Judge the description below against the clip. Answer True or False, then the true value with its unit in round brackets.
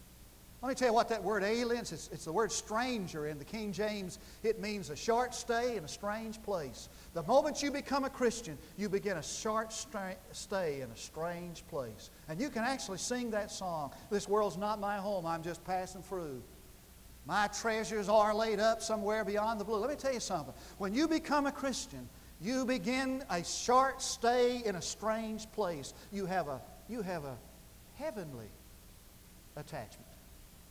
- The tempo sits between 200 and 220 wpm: False (185 wpm)